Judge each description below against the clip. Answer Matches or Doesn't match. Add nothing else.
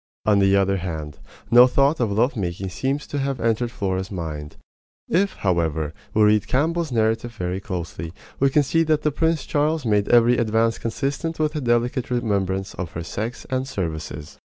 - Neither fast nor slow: Matches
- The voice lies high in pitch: Doesn't match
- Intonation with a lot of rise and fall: Matches